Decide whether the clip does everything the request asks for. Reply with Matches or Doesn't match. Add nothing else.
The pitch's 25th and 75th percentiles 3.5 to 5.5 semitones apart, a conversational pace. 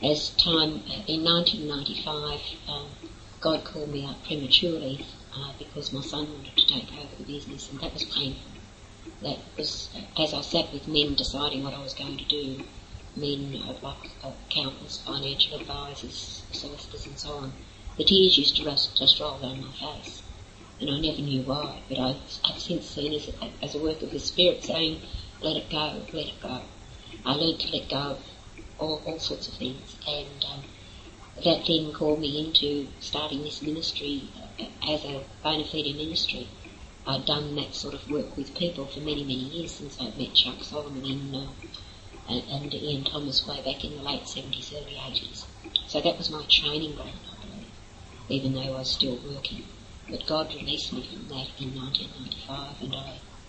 Doesn't match